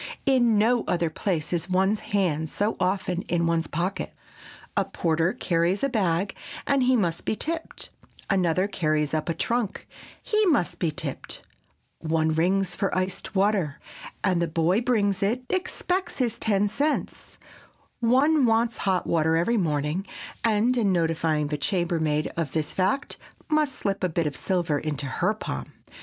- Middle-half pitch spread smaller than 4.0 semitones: No, average, 5.3 semitones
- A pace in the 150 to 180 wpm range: Yes, average, 155 wpm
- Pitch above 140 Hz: Yes, medium, 185 Hz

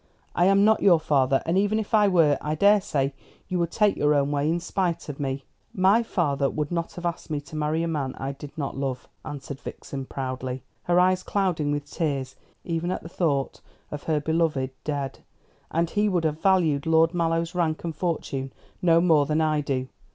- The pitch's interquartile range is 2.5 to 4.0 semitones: Yes, average, 3.6 semitones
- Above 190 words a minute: Yes, fast, 205 wpm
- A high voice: No, medium, 160 Hz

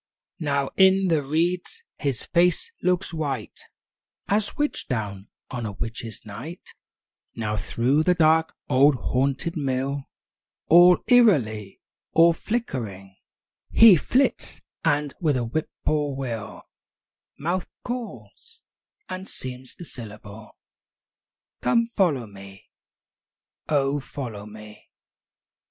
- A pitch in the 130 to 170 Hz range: Yes, medium, 140 Hz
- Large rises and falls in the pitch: Yes, wide, 7.3 semitones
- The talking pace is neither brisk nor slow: No, slow, 105 wpm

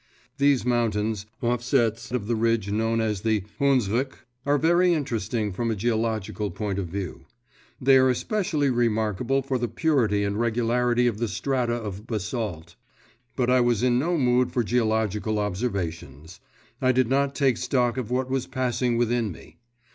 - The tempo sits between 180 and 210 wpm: No, average, 160 wpm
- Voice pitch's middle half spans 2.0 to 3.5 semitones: Yes, average, 3.2 semitones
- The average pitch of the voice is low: Yes, low, 120 Hz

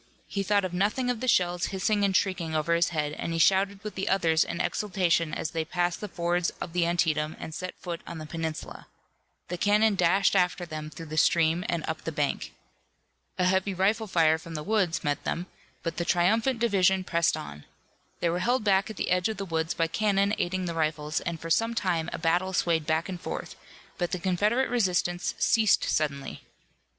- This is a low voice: No, medium, 175 Hz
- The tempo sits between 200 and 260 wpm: Yes, fast, 205 wpm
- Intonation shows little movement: No, average, 3.1 semitones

